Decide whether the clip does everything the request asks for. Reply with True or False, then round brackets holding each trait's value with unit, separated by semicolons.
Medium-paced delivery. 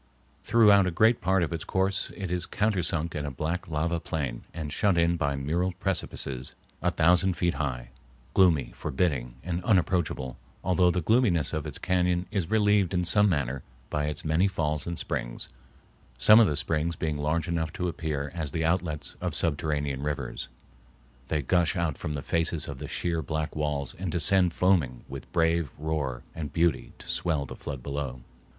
True (180 wpm)